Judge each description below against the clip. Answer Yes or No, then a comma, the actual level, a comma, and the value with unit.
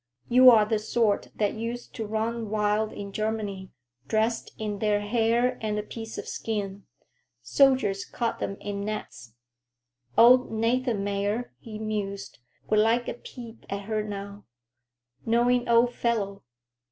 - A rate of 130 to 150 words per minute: Yes, average, 140 wpm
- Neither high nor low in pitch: No, high, 220 Hz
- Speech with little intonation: Yes, narrow, 2.3 semitones